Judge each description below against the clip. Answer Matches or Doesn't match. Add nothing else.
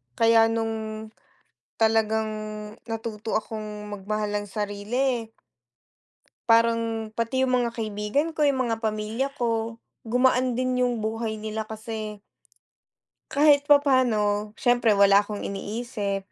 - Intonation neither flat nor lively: Doesn't match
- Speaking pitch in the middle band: Doesn't match